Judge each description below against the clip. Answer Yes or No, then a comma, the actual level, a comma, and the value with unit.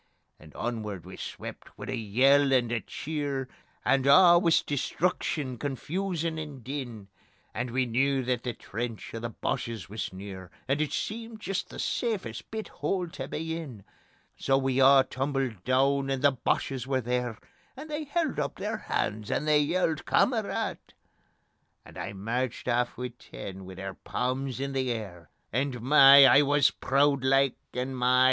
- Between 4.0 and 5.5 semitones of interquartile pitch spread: No, average, 3.4 semitones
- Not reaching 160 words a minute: No, average, 165 wpm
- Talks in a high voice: No, low, 135 Hz